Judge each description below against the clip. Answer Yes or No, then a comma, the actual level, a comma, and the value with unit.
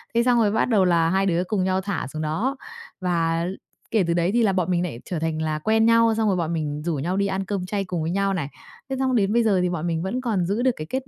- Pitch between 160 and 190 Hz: Yes, medium, 185 Hz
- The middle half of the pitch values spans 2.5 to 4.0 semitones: No, average, 4.5 semitones